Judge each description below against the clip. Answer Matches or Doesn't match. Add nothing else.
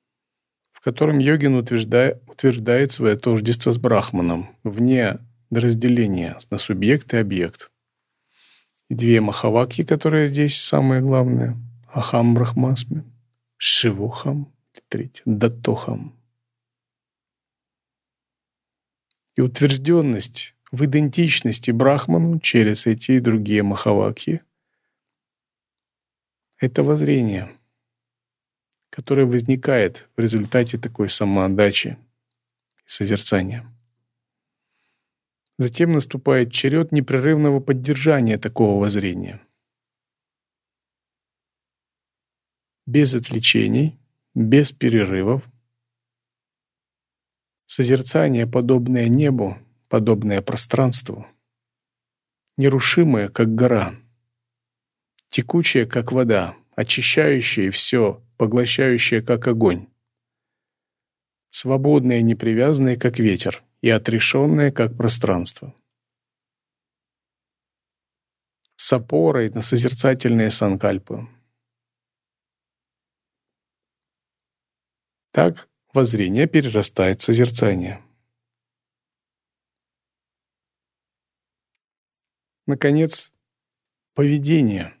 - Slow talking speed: Matches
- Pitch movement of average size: Matches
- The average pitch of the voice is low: Matches